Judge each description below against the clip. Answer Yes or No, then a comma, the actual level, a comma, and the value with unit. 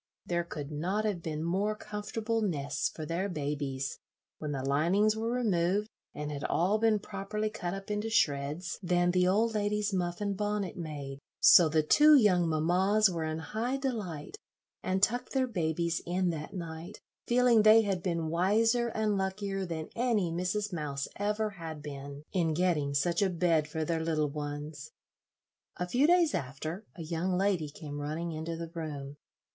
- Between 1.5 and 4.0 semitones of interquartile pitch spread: No, average, 5.0 semitones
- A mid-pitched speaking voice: Yes, medium, 175 Hz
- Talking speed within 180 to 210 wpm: No, average, 170 wpm